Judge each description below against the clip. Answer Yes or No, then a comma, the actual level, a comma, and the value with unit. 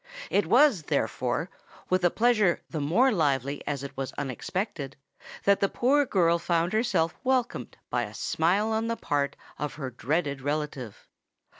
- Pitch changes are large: Yes, wide, 7.0 semitones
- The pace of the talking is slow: No, average, 155 wpm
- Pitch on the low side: No, medium, 170 Hz